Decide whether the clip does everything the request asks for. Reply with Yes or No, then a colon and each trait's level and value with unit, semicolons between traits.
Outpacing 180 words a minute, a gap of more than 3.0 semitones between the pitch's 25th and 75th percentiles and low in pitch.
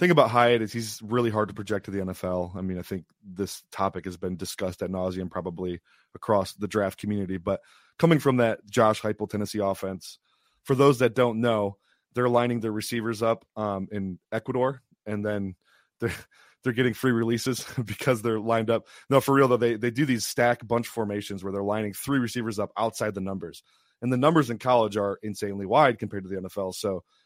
Yes: fast, 205 wpm; average, 3.6 semitones; low, 110 Hz